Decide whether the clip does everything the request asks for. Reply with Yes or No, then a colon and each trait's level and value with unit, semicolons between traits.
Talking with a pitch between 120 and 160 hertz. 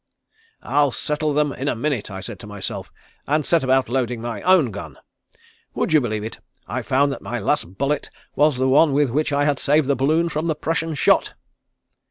Yes: medium, 140 Hz